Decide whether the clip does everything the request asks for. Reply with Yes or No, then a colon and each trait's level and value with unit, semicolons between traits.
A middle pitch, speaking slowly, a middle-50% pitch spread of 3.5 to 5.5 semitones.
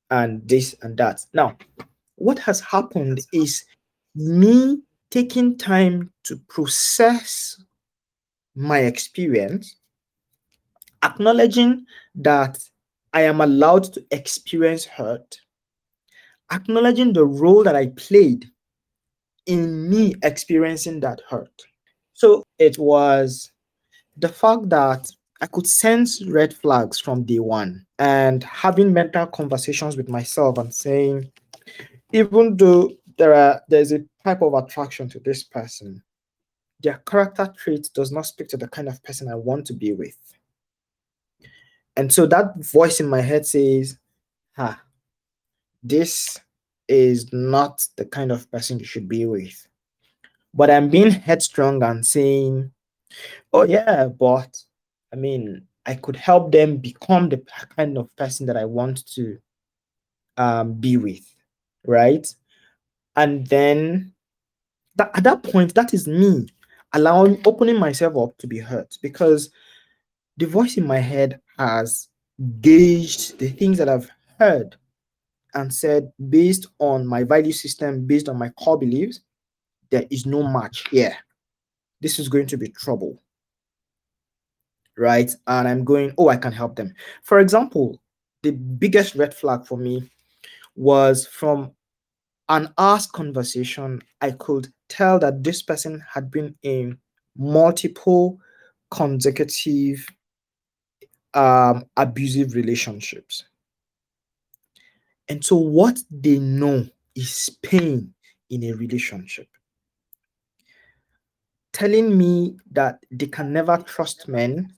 Yes: medium, 145 Hz; slow, 125 wpm; average, 5.2 semitones